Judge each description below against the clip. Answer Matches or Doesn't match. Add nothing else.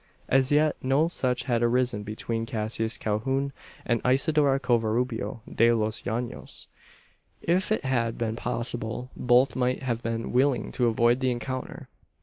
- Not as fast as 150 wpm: Matches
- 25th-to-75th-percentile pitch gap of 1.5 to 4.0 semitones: Matches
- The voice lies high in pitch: Doesn't match